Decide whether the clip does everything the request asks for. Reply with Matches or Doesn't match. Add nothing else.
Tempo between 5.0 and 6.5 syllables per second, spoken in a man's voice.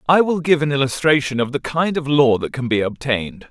Matches